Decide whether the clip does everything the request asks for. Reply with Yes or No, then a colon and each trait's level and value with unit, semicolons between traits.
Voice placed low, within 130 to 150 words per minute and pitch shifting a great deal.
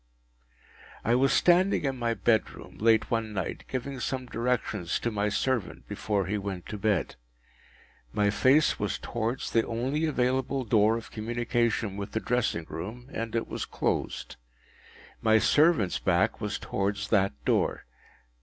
No: low, 115 Hz; average, 145 wpm; average, 3.4 semitones